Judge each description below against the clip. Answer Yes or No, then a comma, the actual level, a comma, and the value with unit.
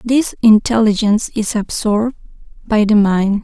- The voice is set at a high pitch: Yes, high, 215 Hz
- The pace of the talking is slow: Yes, slow, 120 wpm